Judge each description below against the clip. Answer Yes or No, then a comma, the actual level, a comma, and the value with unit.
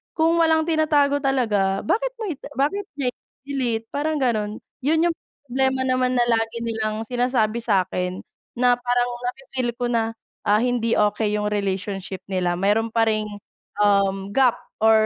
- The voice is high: Yes, high, 240 Hz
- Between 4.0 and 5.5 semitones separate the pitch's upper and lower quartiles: Yes, average, 4.3 semitones